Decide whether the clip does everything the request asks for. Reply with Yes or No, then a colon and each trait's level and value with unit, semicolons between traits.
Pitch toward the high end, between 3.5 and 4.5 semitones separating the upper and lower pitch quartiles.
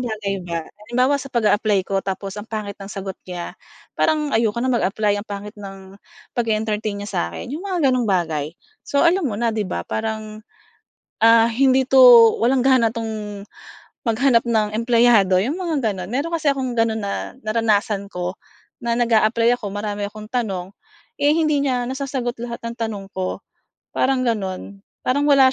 Yes: high, 225 Hz; average, 3.8 semitones